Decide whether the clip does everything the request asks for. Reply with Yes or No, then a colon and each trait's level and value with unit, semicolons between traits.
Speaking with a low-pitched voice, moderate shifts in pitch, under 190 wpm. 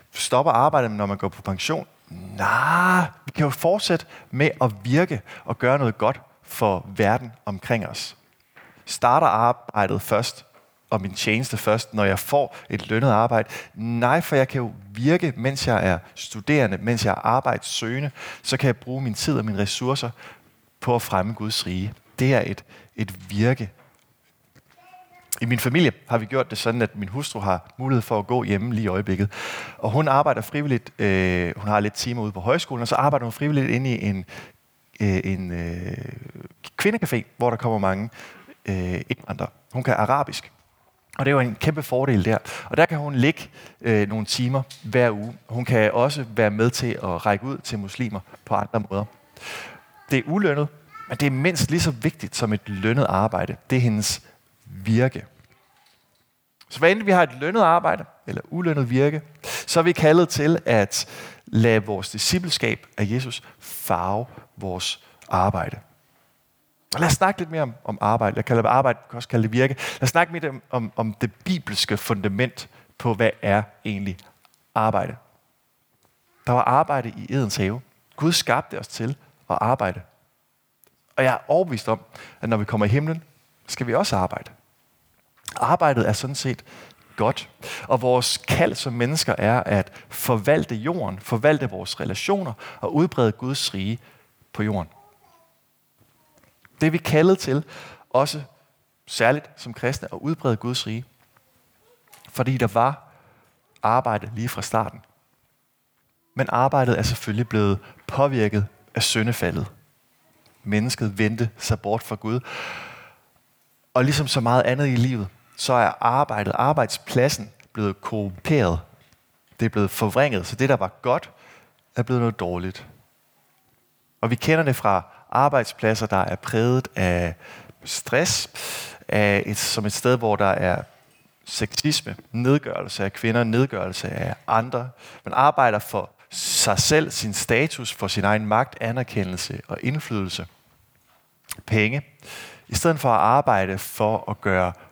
Yes: low, 120 Hz; average, 4.4 semitones; average, 160 wpm